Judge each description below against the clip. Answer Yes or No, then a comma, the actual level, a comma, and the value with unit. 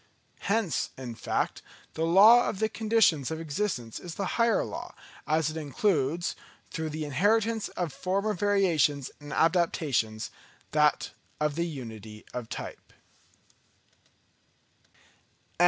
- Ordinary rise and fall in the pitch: No, wide, 5.9 semitones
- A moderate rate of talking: No, slow, 115 wpm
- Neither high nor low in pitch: Yes, medium, 160 Hz